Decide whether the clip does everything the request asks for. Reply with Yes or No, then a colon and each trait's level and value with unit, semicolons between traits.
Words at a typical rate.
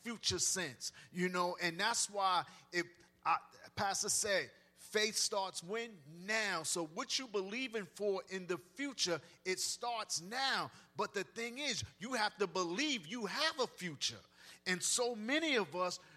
Yes: average, 155 wpm